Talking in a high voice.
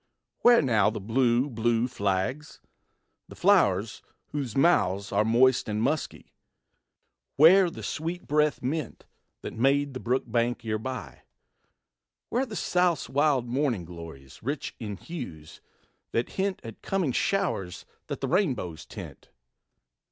No: low, 125 Hz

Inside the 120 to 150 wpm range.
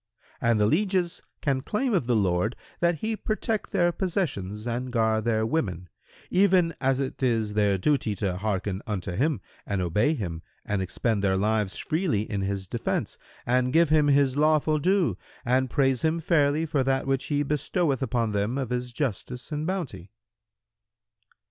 No: average, 165 wpm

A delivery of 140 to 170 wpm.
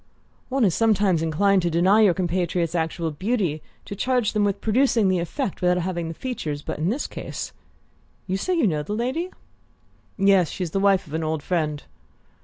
No: average, 190 wpm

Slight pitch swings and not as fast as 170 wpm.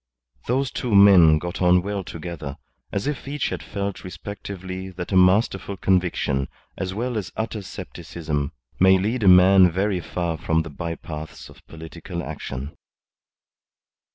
No: average, 3.2 semitones; average, 150 wpm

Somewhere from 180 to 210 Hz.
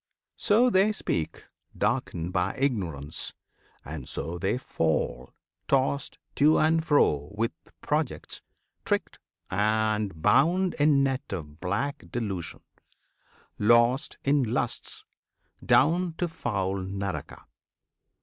No: low, 110 Hz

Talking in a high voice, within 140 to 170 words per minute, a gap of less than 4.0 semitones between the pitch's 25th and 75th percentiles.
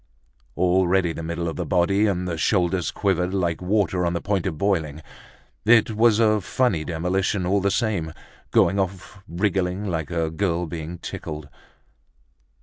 No: very low, 90 Hz; average, 155 wpm; average, 2.9 semitones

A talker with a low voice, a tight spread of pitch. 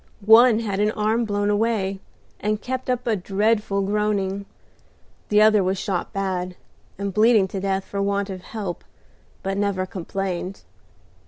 No: high, 200 Hz; narrow, 1.8 semitones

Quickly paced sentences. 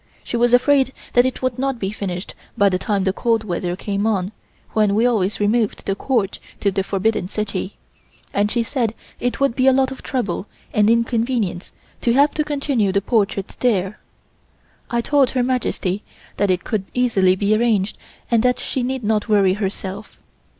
No: average, 185 wpm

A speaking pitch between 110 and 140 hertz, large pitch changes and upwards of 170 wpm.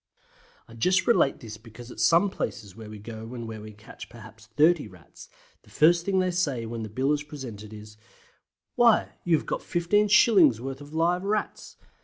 Yes: low, 135 Hz; wide, 7.8 semitones; average, 190 wpm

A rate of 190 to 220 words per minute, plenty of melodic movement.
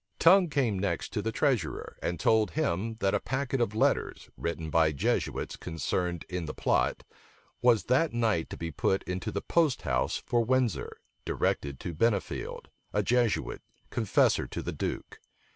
No: average, 160 wpm; wide, 6.3 semitones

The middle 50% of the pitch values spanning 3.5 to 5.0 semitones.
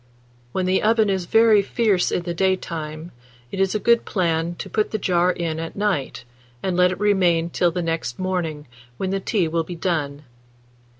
No: average, 2.8 semitones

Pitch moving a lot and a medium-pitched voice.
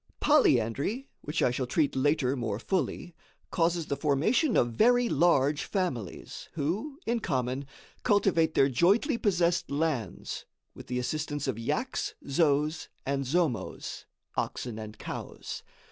Yes: wide, 5.7 semitones; medium, 150 Hz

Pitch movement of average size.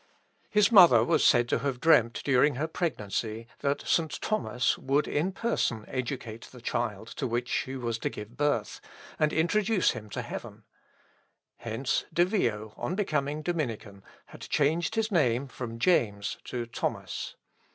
No: wide, 5.9 semitones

